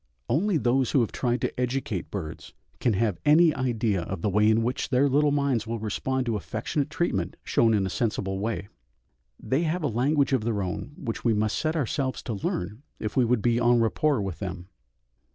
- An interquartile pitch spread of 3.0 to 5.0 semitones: Yes, average, 4.5 semitones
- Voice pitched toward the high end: No, low, 120 Hz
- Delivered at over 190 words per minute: Yes, fast, 205 wpm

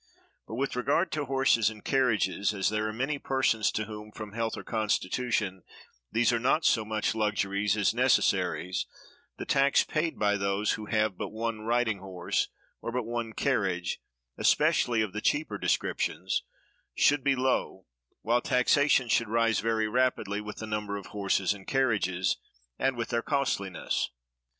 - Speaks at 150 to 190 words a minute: Yes, average, 160 wpm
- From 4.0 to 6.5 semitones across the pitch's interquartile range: No, average, 3.4 semitones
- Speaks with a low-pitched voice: Yes, low, 110 Hz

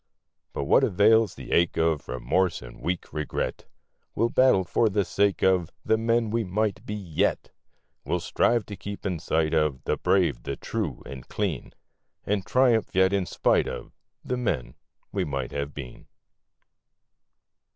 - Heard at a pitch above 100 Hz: No, very low, 95 Hz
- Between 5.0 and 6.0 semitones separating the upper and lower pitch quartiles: Yes, wide, 5.6 semitones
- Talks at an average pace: Yes, average, 160 wpm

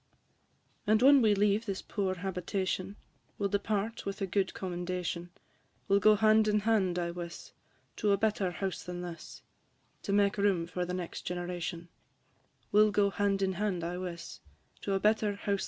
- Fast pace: No, average, 170 wpm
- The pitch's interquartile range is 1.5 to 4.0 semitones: Yes, narrow, 2.5 semitones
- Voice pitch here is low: No, high, 195 Hz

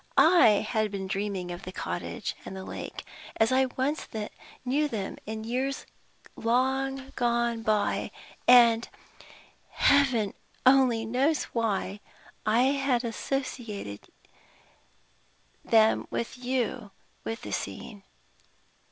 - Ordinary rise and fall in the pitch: Yes, average, 3.4 semitones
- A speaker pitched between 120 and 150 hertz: No, high, 235 Hz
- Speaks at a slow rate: Yes, slow, 100 wpm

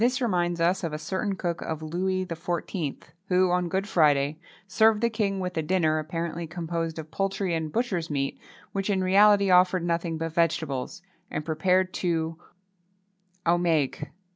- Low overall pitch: No, medium, 175 Hz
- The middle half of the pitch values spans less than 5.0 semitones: Yes, average, 2.7 semitones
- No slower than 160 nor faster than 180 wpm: Yes, average, 165 wpm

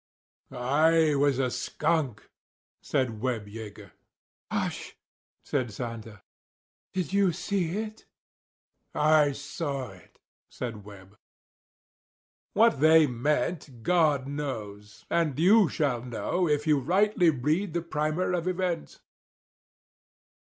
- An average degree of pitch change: No, wide, 5.7 semitones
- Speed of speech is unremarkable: No, slow, 105 wpm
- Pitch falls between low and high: Yes, medium, 145 Hz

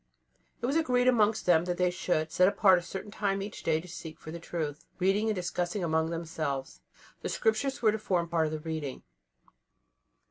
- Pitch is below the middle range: No, medium, 180 Hz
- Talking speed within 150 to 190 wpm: No, average, 200 wpm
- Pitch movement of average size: Yes, average, 4.5 semitones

